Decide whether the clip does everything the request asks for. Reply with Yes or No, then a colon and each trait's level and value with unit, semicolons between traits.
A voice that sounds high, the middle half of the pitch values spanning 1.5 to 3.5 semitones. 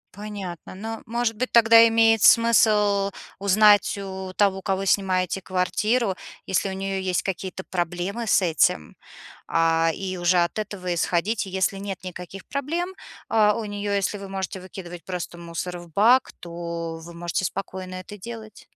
Yes: high, 195 Hz; average, 2.8 semitones